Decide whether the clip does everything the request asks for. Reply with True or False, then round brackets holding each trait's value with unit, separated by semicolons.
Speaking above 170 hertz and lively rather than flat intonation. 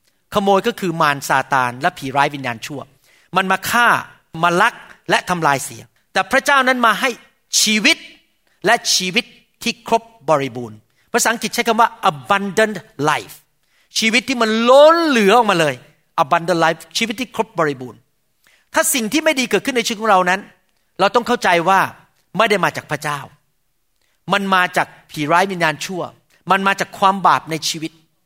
True (190 Hz; 6.2 semitones)